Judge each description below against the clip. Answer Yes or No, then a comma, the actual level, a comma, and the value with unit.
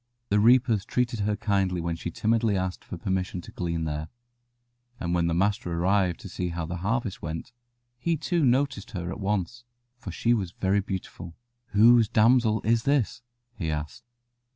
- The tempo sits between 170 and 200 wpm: Yes, average, 175 wpm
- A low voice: Yes, low, 100 Hz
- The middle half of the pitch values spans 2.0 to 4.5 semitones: No, average, 4.9 semitones